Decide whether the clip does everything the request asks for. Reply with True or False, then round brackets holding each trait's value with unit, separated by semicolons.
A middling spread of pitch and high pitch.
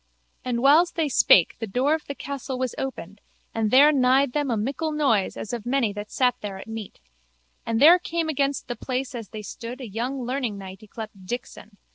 True (4.2 semitones; 250 Hz)